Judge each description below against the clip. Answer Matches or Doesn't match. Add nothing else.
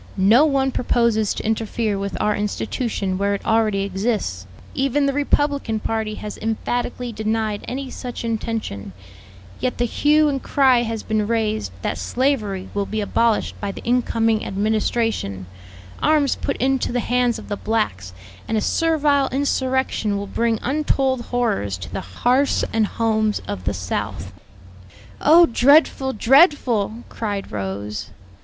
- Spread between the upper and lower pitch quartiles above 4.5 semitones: Doesn't match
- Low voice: Doesn't match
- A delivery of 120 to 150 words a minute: Matches